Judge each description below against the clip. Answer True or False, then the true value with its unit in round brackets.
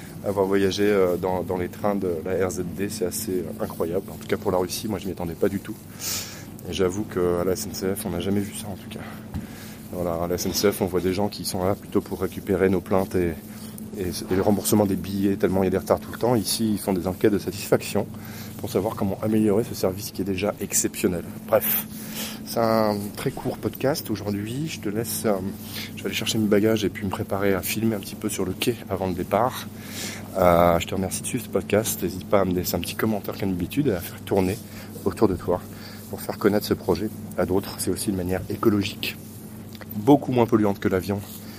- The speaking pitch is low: True (100 Hz)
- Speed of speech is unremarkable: False (230 wpm)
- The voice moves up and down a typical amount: False (2.2 semitones)